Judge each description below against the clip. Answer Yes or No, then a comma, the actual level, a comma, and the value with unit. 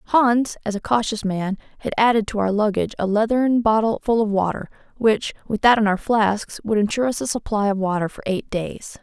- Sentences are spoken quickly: Yes, fast, 215 wpm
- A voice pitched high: Yes, high, 215 Hz